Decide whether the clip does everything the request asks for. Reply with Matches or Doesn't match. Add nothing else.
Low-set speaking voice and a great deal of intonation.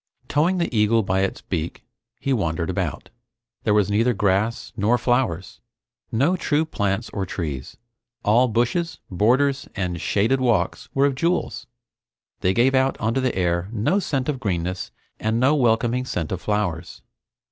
Matches